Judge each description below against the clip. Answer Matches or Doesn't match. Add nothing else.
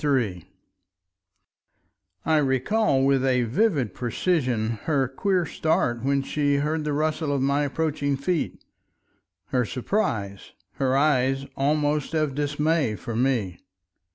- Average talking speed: Doesn't match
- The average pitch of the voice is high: Doesn't match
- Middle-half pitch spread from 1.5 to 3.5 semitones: Matches